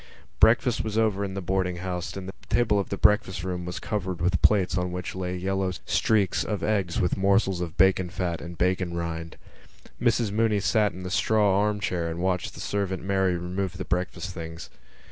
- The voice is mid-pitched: No, very low, 95 Hz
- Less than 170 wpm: No, average, 200 wpm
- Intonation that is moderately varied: No, narrow, 2.2 semitones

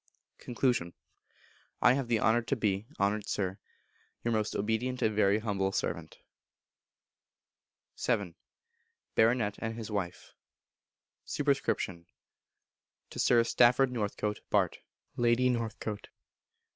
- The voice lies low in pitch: Yes, low, 110 Hz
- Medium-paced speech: No, slow, 105 wpm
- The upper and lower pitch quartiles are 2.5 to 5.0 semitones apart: Yes, average, 2.8 semitones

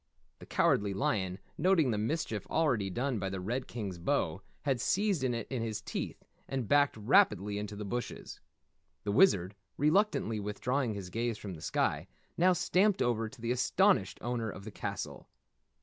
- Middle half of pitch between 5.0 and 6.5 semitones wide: Yes, wide, 5.6 semitones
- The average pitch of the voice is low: Yes, low, 115 Hz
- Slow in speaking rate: No, average, 165 wpm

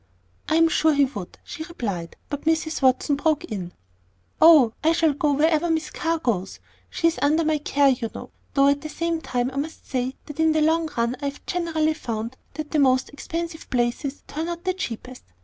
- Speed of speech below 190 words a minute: No, average, 200 wpm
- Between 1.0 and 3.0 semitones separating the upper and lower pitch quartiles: No, average, 3.8 semitones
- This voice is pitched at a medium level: No, very high, 295 Hz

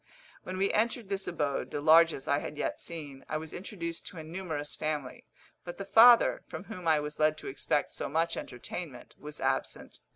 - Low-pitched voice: No, medium, 160 Hz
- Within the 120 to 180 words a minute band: No, average, 195 wpm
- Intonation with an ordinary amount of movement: Yes, average, 3.9 semitones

